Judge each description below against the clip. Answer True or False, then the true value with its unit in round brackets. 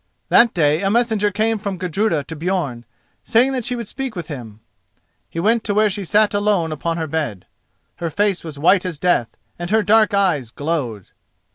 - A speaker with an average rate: True (190 wpm)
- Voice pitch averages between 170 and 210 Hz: True (185 Hz)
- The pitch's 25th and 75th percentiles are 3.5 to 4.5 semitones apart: False (5.4 semitones)